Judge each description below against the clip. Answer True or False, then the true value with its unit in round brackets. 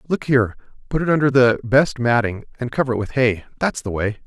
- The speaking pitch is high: False (125 Hz)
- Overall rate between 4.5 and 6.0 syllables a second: True (5.9 syllables/s)